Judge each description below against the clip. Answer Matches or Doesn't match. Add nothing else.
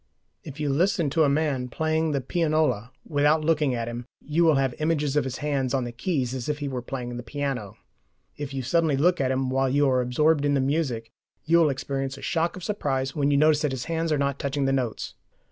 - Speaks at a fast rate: Matches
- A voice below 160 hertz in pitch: Matches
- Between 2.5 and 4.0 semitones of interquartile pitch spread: Matches